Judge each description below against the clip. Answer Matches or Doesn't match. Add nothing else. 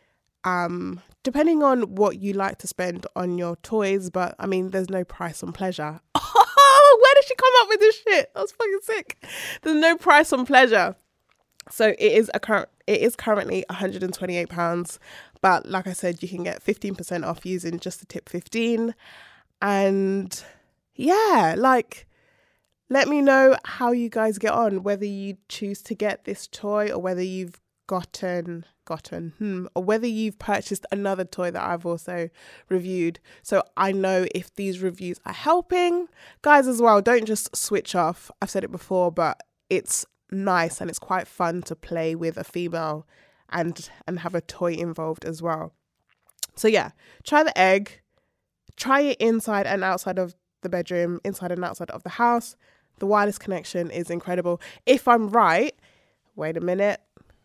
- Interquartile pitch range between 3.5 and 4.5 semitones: Doesn't match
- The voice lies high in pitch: Matches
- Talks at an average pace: Matches